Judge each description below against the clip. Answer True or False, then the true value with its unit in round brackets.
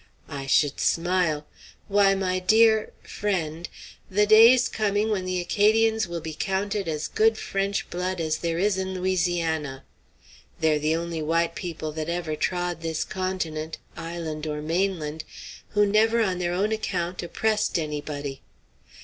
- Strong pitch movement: False (3.9 semitones)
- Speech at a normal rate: True (145 wpm)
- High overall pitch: False (175 Hz)